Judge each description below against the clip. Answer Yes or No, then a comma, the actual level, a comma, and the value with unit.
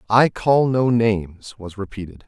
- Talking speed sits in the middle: Yes, average, 160 wpm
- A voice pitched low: Yes, low, 105 Hz